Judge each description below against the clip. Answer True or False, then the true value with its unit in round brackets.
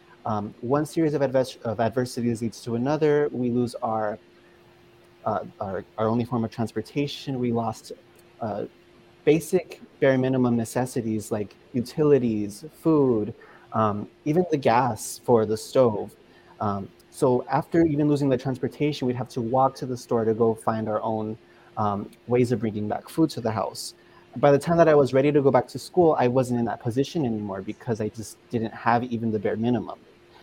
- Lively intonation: False (3.8 semitones)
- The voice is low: True (120 Hz)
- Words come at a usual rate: True (180 wpm)